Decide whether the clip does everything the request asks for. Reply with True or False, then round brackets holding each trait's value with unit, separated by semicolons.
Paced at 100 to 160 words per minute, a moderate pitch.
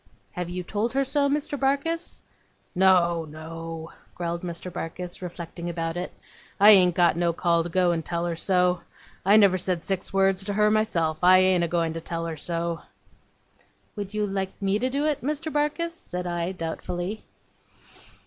False (175 wpm; 180 Hz)